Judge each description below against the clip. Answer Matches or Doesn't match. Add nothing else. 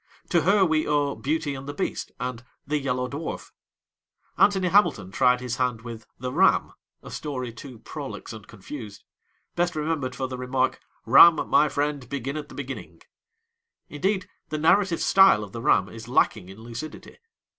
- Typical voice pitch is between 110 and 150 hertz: Matches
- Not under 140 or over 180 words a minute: Matches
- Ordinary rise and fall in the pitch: Matches